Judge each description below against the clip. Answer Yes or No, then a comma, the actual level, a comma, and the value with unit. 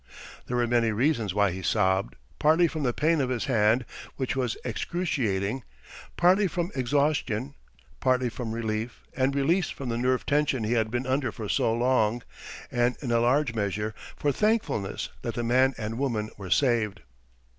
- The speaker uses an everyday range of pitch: Yes, average, 4.0 semitones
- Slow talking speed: No, average, 165 wpm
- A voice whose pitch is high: No, low, 120 Hz